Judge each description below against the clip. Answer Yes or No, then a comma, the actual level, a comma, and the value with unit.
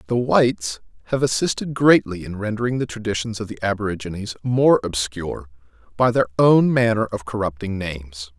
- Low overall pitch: Yes, low, 105 Hz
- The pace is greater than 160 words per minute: No, average, 150 wpm